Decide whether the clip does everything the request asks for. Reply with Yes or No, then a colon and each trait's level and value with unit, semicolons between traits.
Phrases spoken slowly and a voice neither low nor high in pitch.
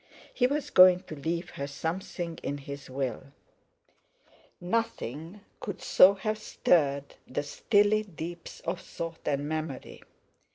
Yes: slow, 125 wpm; medium, 170 Hz